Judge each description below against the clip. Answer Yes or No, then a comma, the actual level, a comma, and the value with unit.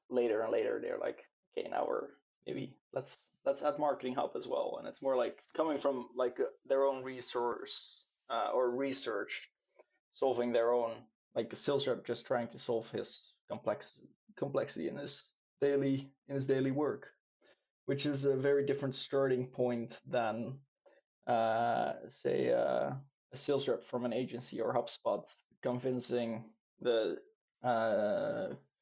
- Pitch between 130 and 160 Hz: Yes, low, 135 Hz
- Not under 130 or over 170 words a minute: Yes, average, 150 wpm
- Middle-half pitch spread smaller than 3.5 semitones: Yes, narrow, 2.4 semitones